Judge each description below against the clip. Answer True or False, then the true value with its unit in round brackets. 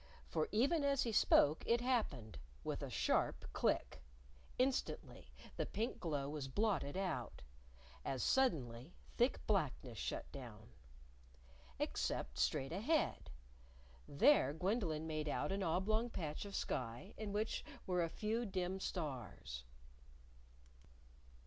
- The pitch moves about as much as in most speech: False (8.0 semitones)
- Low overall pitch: False (180 Hz)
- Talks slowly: True (120 wpm)